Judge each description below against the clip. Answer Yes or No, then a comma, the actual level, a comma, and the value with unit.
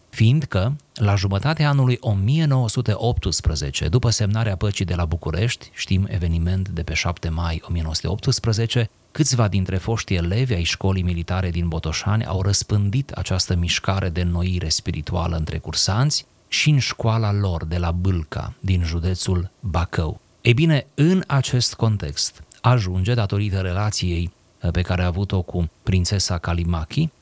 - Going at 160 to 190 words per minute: No, average, 135 wpm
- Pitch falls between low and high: No, very low, 95 Hz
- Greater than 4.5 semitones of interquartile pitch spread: Yes, average, 4.9 semitones